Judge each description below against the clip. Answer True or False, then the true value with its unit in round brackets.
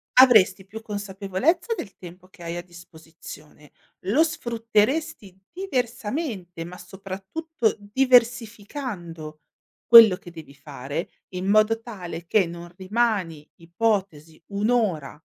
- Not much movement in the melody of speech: False (5.1 semitones)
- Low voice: False (195 Hz)